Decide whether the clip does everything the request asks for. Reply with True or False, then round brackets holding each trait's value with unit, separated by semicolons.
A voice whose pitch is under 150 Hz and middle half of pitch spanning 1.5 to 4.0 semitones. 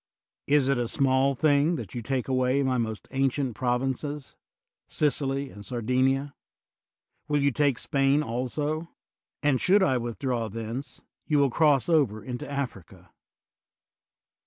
True (135 Hz; 2.7 semitones)